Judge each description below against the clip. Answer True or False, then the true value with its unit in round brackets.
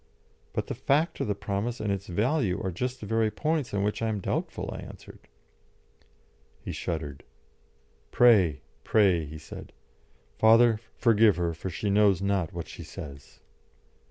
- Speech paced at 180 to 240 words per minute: False (155 wpm)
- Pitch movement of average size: True (4.4 semitones)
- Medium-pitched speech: False (100 Hz)